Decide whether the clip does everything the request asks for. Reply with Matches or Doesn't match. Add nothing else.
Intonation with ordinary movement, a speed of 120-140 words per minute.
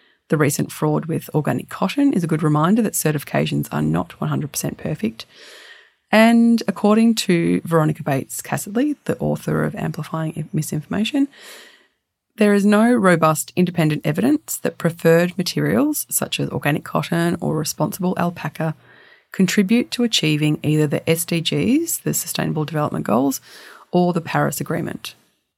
Doesn't match